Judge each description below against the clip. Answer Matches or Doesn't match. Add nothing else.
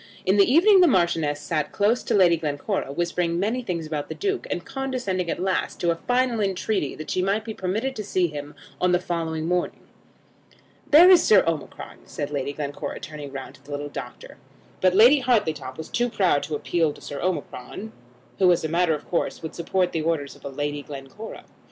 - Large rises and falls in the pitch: Matches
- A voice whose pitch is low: Doesn't match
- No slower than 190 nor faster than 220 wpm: Matches